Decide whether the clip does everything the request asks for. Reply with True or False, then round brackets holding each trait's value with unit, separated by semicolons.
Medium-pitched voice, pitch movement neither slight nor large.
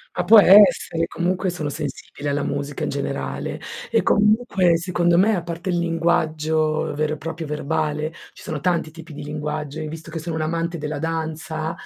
False (160 Hz; 2.1 semitones)